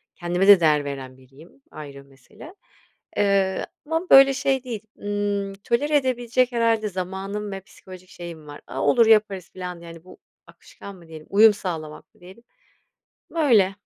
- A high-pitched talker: Yes, high, 195 Hz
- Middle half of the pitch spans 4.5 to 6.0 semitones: Yes, average, 5.1 semitones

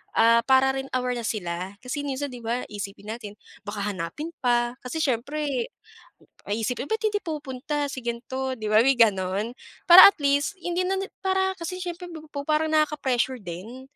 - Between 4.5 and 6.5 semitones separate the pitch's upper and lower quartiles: Yes, average, 5.1 semitones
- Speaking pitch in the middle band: No, very high, 260 Hz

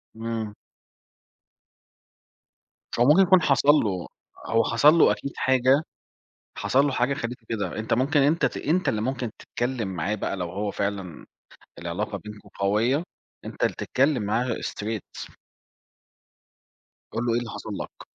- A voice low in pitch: Yes, low, 115 Hz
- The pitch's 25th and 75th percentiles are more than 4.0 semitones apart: Yes, average, 4.5 semitones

